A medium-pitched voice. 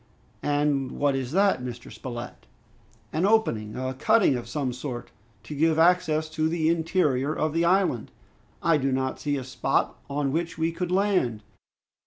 Yes: medium, 150 Hz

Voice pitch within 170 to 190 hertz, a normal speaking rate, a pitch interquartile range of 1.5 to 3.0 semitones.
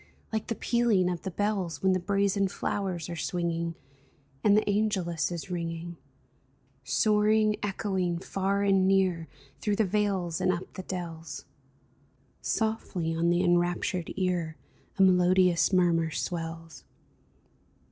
No: medium, 185 Hz; slow, 130 wpm; average, 2.7 semitones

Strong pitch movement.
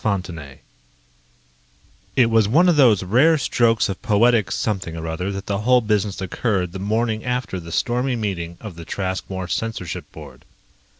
No: average, 4.1 semitones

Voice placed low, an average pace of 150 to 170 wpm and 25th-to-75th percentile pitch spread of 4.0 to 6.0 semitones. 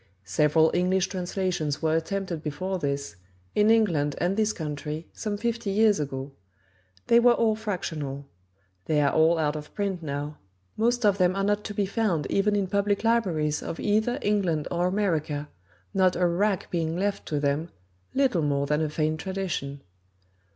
No: medium, 180 Hz; average, 165 wpm; average, 5.2 semitones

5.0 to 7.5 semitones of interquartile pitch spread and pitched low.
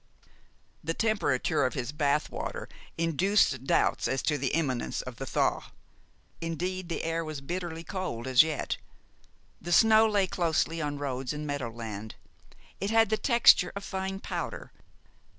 No: wide, 5.6 semitones; medium, 160 Hz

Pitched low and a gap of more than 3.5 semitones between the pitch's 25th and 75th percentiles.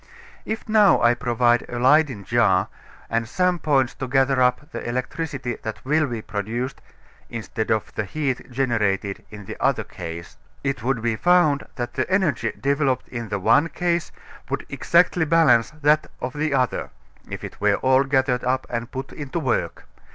Yes: low, 130 Hz; average, 4.1 semitones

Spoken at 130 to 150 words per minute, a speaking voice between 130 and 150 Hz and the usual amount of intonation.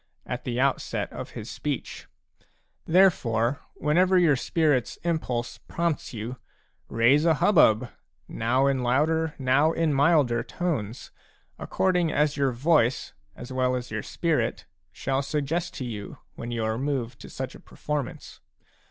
Yes: average, 140 wpm; low, 135 Hz; average, 4.8 semitones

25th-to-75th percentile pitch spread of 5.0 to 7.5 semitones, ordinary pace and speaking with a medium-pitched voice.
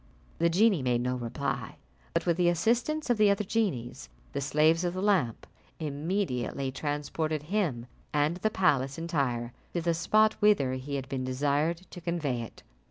Yes: wide, 5.6 semitones; average, 165 wpm; medium, 155 Hz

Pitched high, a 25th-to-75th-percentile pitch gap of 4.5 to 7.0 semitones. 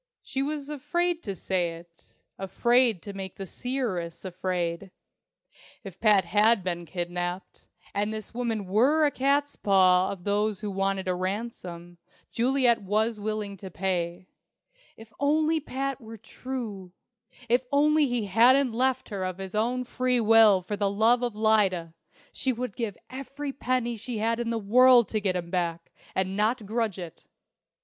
Yes: high, 215 Hz; average, 4.8 semitones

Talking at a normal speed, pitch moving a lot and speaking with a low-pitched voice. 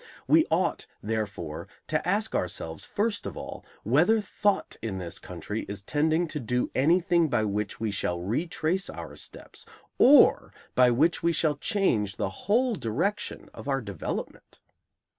Yes: average, 150 wpm; wide, 8.9 semitones; low, 130 Hz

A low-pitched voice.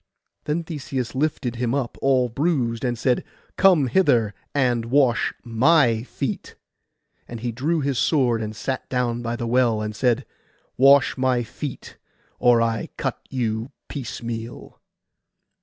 Yes: low, 125 Hz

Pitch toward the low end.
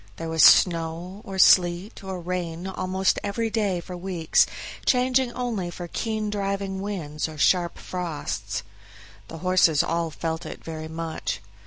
No: medium, 180 Hz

